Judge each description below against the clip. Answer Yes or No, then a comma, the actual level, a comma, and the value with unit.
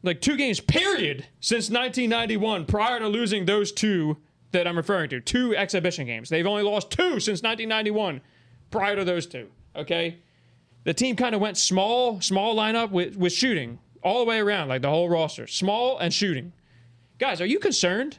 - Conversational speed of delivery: Yes, average, 180 wpm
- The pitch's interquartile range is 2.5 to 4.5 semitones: No, average, 5.2 semitones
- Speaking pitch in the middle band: No, high, 195 Hz